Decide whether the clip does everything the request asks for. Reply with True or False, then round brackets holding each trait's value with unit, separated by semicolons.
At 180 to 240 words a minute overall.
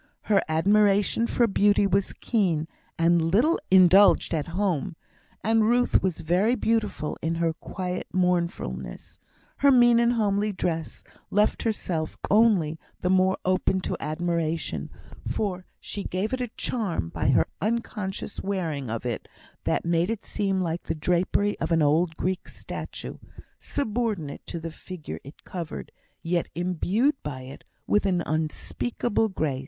False (145 wpm)